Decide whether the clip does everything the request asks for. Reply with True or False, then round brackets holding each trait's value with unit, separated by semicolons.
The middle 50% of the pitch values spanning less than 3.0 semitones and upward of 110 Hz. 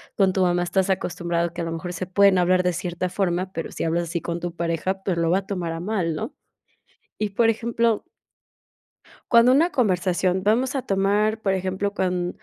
True (2.6 semitones; 185 Hz)